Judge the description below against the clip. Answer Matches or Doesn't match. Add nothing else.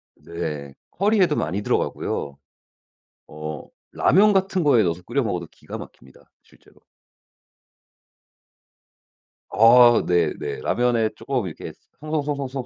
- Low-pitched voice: Matches